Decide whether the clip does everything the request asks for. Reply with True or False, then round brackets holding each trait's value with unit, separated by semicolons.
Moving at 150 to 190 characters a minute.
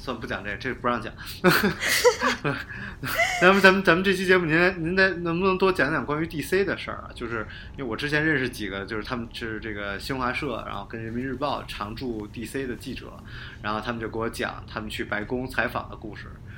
False (325 characters per minute)